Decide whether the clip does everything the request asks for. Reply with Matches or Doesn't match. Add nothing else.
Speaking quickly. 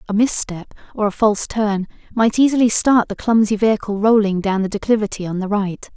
Doesn't match